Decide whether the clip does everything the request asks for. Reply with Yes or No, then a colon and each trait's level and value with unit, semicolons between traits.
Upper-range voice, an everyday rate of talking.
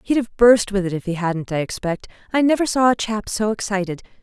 No: high, 210 Hz; fast, 240 wpm